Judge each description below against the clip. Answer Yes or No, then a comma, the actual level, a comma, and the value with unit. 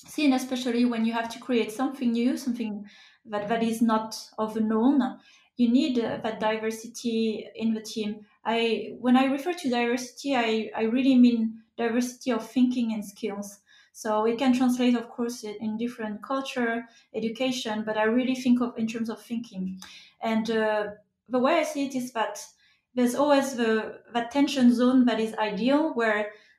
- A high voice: Yes, high, 230 Hz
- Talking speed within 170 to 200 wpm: Yes, average, 175 wpm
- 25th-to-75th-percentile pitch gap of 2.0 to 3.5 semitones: Yes, narrow, 2.4 semitones